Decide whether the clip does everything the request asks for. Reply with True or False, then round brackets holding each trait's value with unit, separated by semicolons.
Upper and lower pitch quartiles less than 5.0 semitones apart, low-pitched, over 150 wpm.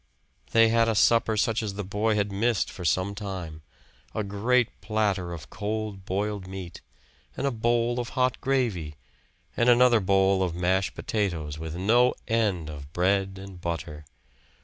True (3.8 semitones; 100 Hz; 160 wpm)